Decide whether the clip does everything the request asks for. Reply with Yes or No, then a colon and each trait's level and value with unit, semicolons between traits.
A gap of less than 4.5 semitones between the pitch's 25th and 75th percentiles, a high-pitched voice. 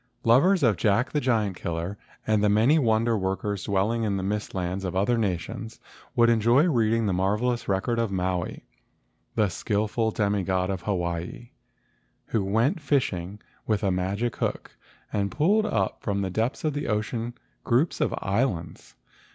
No: average, 3.6 semitones; low, 105 Hz